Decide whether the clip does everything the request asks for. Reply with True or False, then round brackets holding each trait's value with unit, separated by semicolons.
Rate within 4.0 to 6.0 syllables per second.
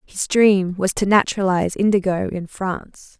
True (4.9 syllables/s)